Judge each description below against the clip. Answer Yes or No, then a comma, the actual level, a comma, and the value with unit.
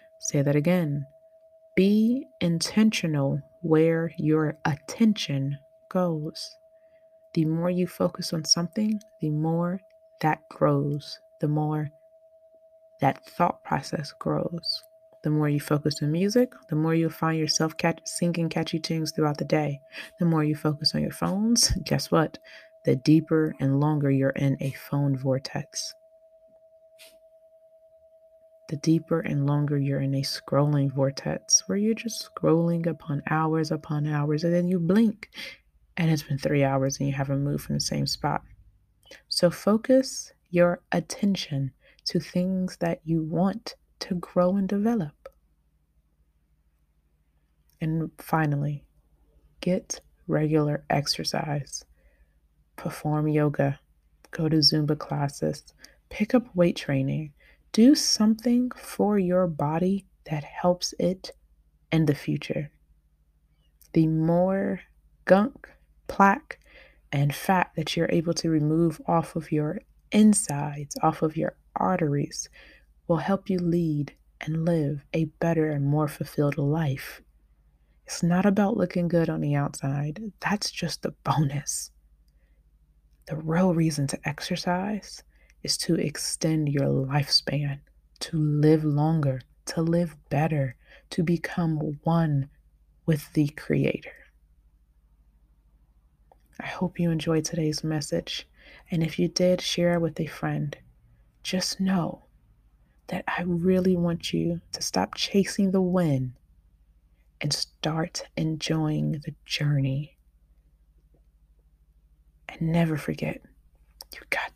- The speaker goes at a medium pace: No, slow, 125 wpm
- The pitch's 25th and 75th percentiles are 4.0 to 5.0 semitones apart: Yes, average, 4.6 semitones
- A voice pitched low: No, medium, 160 Hz